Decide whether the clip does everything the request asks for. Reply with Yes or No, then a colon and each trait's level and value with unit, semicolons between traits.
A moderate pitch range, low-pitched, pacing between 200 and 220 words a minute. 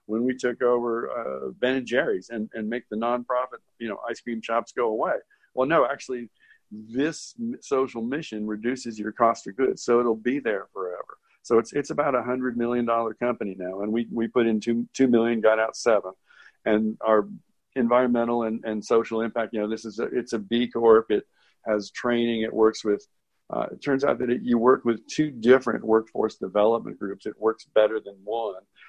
No: narrow, 1.9 semitones; low, 115 Hz; fast, 205 wpm